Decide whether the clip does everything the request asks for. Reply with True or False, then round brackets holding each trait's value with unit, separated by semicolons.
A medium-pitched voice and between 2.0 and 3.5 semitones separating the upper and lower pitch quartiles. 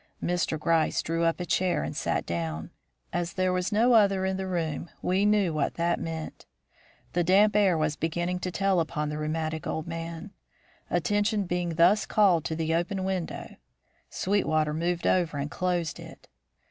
True (175 Hz; 2.8 semitones)